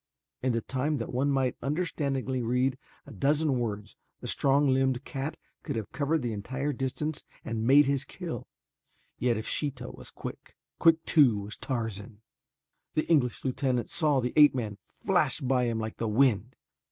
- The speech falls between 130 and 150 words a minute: No, average, 165 wpm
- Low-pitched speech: Yes, low, 130 Hz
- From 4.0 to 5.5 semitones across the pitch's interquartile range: No, average, 3.4 semitones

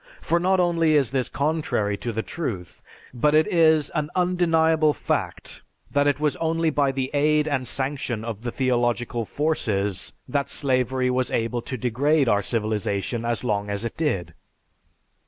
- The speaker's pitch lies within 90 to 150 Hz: Yes, low, 135 Hz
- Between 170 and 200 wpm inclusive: No, average, 160 wpm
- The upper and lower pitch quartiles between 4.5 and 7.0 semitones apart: Yes, average, 4.8 semitones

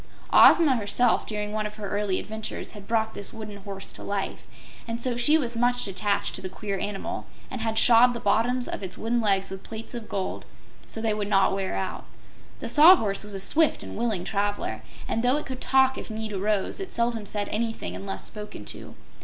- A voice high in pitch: Yes, high, 215 Hz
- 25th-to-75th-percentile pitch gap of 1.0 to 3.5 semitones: Yes, average, 2.9 semitones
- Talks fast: Yes, fast, 210 wpm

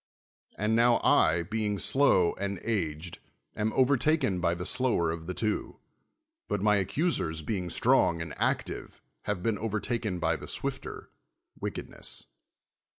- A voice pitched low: Yes, low, 100 Hz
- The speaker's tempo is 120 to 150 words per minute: Yes, slow, 135 wpm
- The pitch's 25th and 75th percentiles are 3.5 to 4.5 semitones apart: No, average, 4.9 semitones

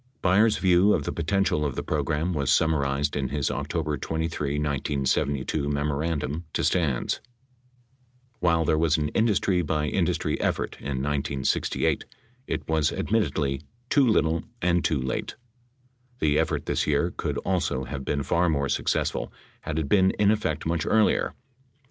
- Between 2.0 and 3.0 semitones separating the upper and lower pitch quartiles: No, average, 3.6 semitones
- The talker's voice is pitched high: No, very low, 75 Hz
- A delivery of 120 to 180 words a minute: Yes, average, 150 wpm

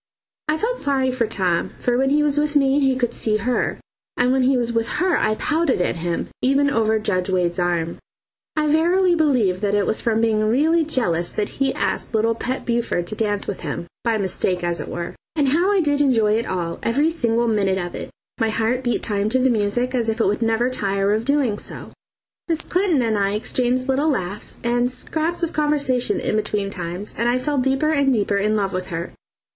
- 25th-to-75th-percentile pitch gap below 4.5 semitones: No, average, 5.1 semitones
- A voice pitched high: Yes, high, 235 Hz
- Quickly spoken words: Yes, fast, 215 wpm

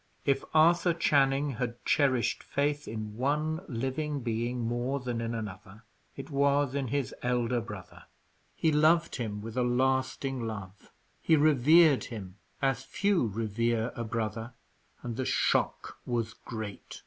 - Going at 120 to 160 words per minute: Yes, average, 140 wpm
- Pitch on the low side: Yes, low, 125 Hz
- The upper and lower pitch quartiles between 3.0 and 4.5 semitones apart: Yes, average, 3.8 semitones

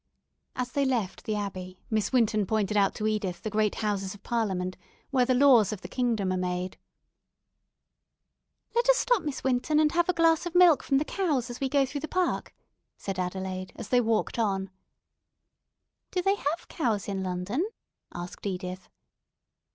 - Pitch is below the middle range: No, high, 220 Hz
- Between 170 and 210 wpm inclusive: Yes, average, 175 wpm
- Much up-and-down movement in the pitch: Yes, wide, 6.6 semitones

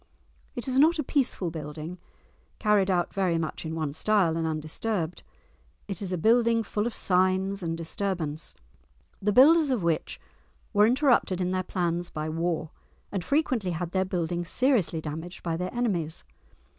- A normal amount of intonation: Yes, average, 4.6 semitones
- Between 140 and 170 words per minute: Yes, average, 160 wpm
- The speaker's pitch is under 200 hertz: Yes, medium, 185 Hz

